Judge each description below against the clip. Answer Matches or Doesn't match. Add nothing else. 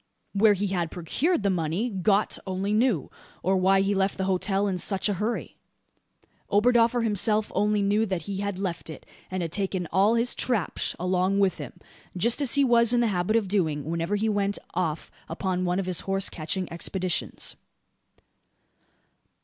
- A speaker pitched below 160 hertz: Doesn't match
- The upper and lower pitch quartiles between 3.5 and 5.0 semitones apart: Doesn't match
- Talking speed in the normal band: Matches